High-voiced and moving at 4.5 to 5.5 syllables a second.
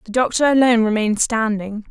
No: high, 225 Hz; 6.2 syllables/s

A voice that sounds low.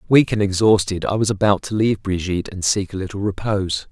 Yes: low, 100 Hz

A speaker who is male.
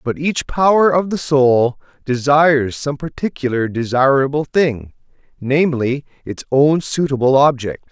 Yes: male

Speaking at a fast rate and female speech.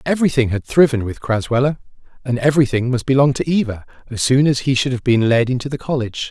No: fast, 210 wpm; male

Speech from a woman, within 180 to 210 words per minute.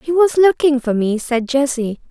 Yes: female; average, 200 wpm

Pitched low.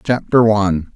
Yes: low, 105 Hz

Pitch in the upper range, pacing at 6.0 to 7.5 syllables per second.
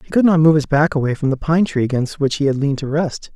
No: medium, 150 Hz; 6.5 syllables/s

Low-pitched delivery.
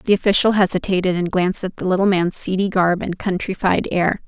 No: medium, 185 Hz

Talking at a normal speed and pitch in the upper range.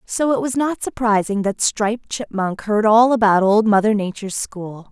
Yes: average, 185 wpm; high, 215 Hz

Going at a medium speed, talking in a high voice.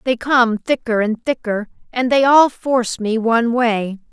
Yes: average, 175 wpm; high, 235 Hz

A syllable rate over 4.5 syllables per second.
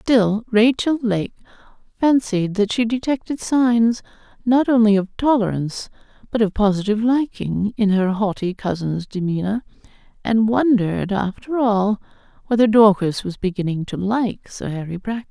Yes: 4.7 syllables/s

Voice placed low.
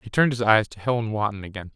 Yes: low, 110 Hz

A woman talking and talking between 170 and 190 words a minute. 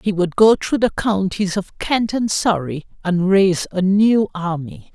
Yes: female; average, 180 wpm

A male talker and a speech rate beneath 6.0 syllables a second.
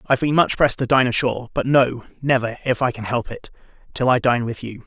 No: male; 6.2 syllables/s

